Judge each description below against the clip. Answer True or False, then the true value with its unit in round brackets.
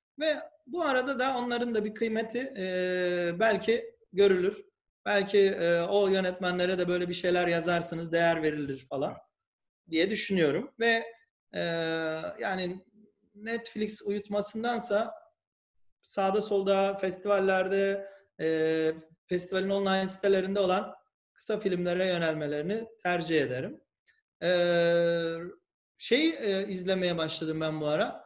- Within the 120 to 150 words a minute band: False (110 wpm)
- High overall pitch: True (195 Hz)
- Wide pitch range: False (4.3 semitones)